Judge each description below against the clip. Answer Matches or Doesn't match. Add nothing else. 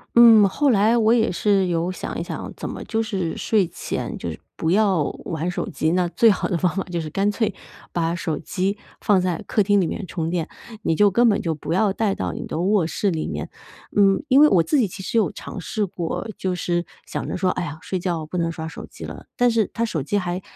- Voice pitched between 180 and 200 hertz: Matches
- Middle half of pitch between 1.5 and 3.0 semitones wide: Doesn't match